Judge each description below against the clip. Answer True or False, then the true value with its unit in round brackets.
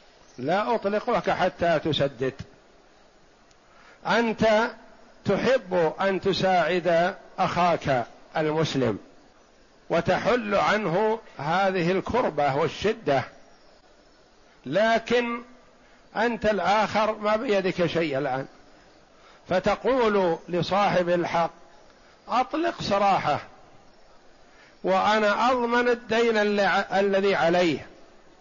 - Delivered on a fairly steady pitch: False (4.1 semitones)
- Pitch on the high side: True (195 Hz)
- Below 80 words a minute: True (70 wpm)